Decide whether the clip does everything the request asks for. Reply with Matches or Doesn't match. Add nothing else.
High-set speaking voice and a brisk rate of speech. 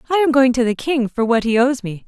Matches